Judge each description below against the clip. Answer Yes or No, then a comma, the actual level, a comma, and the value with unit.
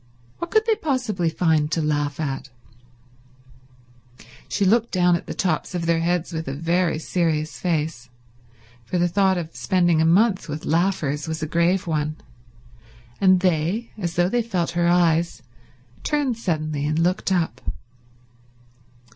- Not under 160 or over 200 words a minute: No, average, 150 wpm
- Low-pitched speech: No, medium, 170 Hz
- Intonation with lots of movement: No, average, 3.0 semitones